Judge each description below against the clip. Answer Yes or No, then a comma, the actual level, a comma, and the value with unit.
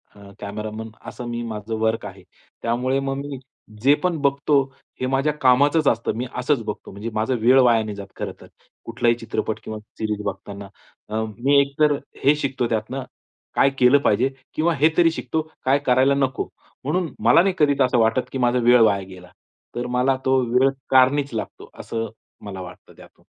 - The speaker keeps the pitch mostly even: No, average, 3.7 semitones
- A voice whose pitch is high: No, low, 125 Hz